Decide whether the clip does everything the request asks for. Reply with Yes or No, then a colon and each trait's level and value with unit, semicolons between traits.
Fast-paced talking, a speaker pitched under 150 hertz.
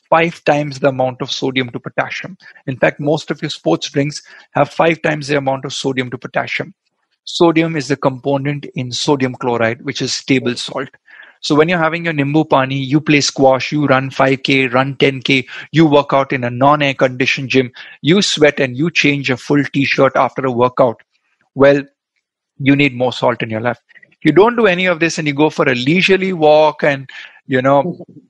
Yes: fast, 200 wpm; medium, 140 Hz